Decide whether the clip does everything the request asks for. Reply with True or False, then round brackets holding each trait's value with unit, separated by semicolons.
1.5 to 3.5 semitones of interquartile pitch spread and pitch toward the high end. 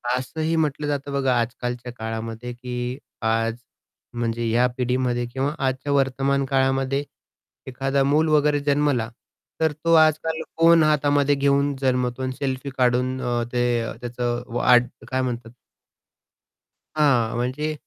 False (2.8 semitones; 130 Hz)